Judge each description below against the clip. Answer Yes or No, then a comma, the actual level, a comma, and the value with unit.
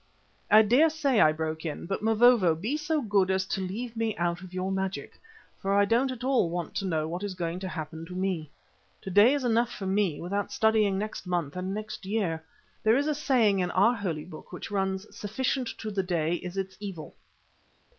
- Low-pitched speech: No, high, 195 Hz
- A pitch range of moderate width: Yes, average, 3.9 semitones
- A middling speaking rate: No, fast, 210 wpm